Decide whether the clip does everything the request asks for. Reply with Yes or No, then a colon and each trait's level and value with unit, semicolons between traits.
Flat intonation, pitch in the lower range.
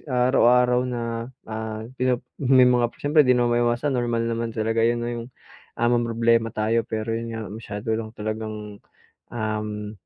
Yes: narrow, 1.8 semitones; low, 115 Hz